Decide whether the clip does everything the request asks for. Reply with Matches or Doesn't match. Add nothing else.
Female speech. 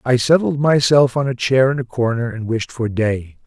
Doesn't match